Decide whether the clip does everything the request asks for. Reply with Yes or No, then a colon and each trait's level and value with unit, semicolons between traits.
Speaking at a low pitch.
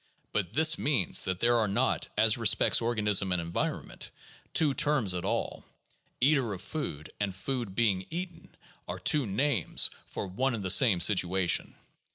Yes: low, 110 Hz